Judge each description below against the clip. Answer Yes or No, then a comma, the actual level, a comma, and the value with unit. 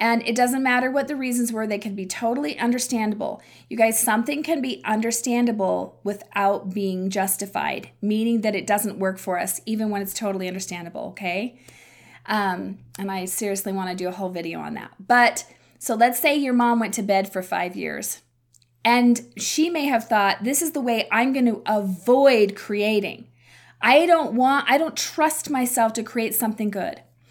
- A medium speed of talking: Yes, average, 180 wpm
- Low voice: No, high, 220 Hz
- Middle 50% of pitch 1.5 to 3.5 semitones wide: No, average, 3.9 semitones